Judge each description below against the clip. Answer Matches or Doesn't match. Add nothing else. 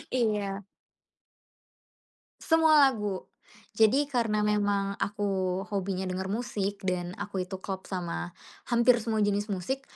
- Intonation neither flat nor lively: Matches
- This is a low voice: Doesn't match